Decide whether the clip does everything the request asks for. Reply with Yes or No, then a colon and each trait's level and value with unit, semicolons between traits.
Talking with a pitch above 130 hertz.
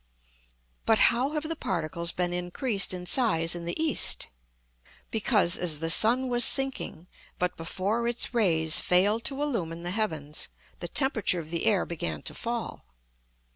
Yes: high, 190 Hz